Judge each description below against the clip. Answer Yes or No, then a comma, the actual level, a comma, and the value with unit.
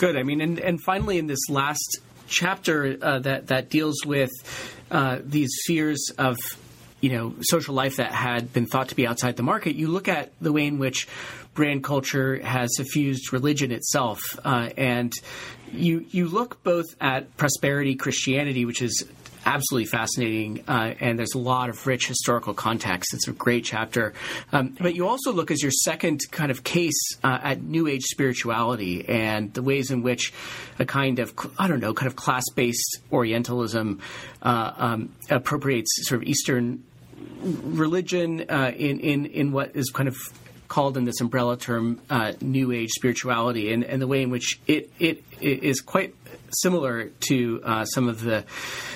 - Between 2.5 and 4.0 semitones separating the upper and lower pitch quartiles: Yes, average, 3.4 semitones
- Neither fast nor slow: Yes, average, 180 wpm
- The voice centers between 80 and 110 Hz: No, low, 130 Hz